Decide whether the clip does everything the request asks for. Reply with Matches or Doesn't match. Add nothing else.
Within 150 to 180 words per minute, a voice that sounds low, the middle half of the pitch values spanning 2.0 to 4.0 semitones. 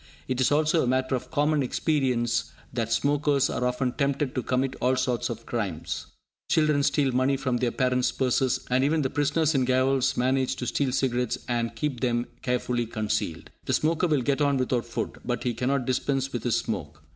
Doesn't match